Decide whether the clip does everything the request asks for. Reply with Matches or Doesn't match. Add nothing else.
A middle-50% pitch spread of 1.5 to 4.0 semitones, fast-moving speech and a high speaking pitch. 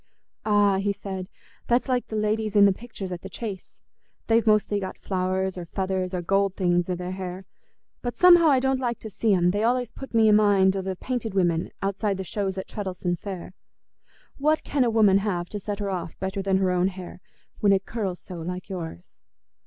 Matches